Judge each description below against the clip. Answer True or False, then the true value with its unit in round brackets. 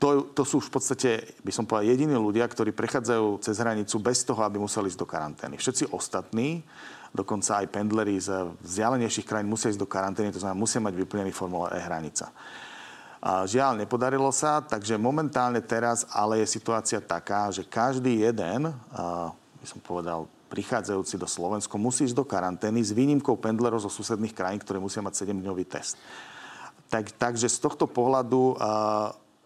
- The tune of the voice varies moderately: True (3.8 semitones)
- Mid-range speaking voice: False (110 Hz)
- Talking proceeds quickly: True (170 wpm)